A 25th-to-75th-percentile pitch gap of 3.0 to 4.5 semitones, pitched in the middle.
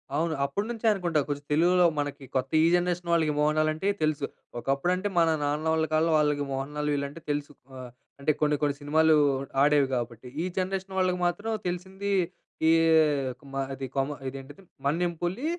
Yes: average, 3.7 semitones; medium, 155 Hz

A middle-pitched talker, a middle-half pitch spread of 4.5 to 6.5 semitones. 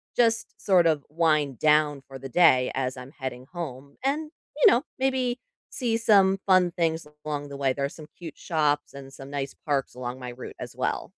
Yes: medium, 150 Hz; wide, 5.5 semitones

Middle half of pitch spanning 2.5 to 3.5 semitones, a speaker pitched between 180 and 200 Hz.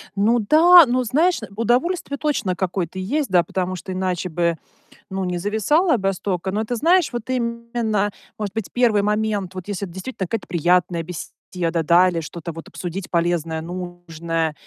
No: average, 4.9 semitones; high, 190 Hz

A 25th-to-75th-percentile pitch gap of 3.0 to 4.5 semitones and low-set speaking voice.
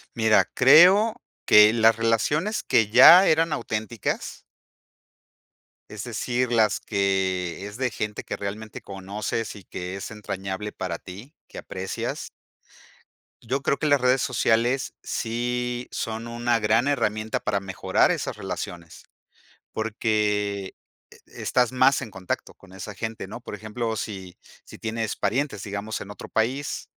Yes: average, 3.4 semitones; low, 110 Hz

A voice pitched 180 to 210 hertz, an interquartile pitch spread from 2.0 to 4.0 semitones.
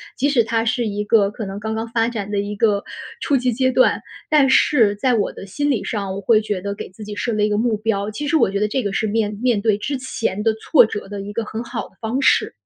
No: high, 220 Hz; average, 2.9 semitones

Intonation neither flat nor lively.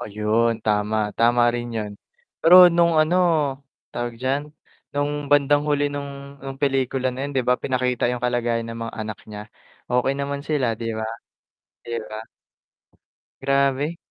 Yes: average, 3.5 semitones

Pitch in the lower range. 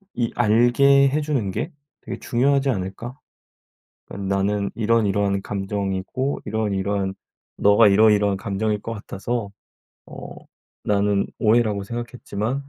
Yes: low, 105 Hz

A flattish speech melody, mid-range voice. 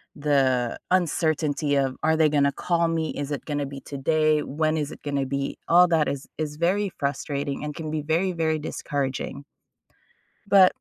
Yes: narrow, 2.3 semitones; medium, 150 Hz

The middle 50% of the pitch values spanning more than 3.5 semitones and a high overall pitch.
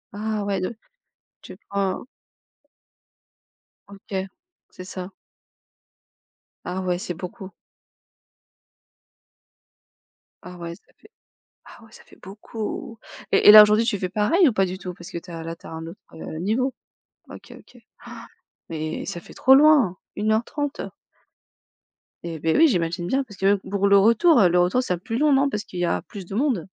Yes: average, 4.2 semitones; high, 195 Hz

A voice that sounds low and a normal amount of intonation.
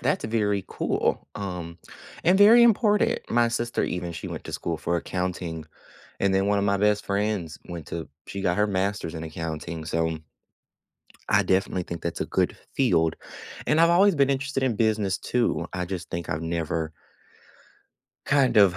No: very low, 95 Hz; wide, 5.7 semitones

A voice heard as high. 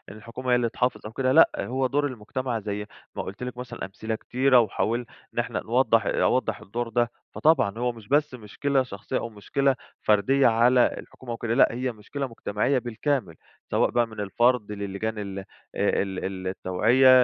No: low, 120 Hz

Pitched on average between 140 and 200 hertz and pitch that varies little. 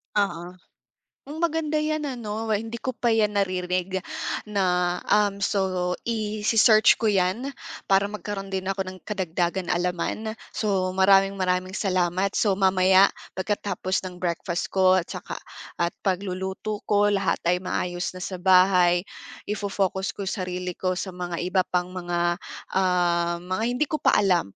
Yes: high, 190 Hz; narrow, 2.3 semitones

